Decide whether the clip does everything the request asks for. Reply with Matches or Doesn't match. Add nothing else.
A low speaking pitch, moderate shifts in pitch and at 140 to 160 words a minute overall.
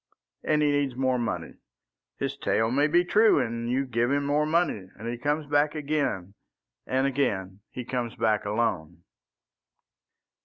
Matches